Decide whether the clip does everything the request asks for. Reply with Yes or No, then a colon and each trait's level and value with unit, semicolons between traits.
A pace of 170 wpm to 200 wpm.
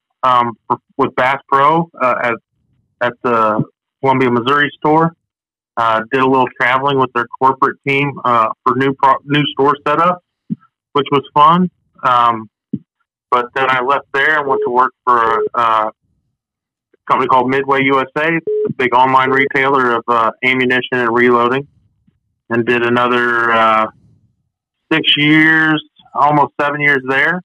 No: average, 150 wpm